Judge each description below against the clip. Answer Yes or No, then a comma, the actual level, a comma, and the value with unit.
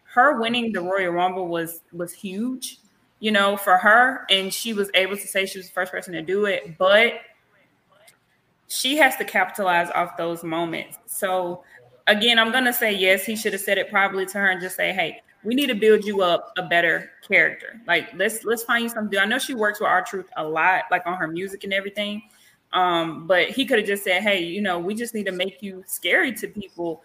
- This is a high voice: Yes, high, 195 Hz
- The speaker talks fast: Yes, fast, 230 wpm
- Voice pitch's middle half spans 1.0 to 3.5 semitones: Yes, average, 3.2 semitones